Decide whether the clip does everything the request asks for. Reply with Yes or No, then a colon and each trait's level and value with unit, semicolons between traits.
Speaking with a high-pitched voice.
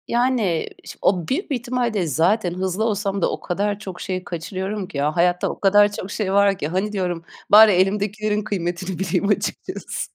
Yes: high, 195 Hz